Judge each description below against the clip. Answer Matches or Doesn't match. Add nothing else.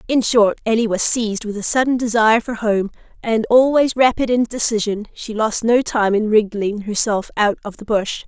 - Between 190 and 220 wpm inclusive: Matches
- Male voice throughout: Doesn't match